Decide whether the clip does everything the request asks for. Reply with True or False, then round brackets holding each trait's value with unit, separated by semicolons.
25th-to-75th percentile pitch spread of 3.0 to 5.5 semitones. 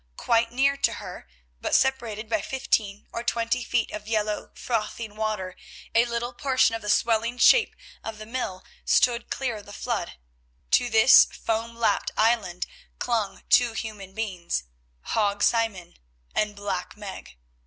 False (2.5 semitones)